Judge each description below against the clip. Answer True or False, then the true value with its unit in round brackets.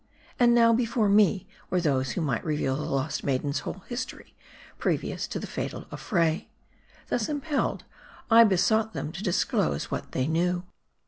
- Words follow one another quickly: False (155 wpm)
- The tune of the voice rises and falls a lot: True (7.1 semitones)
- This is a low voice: False (180 Hz)